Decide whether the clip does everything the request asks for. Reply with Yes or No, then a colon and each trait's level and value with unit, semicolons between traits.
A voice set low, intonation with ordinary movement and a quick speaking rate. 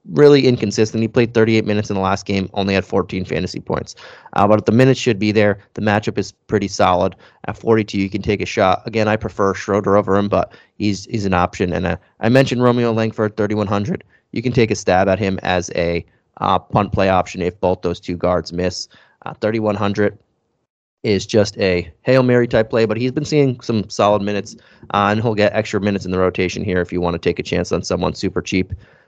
Yes: low, 105 Hz; average, 3.0 semitones; fast, 225 wpm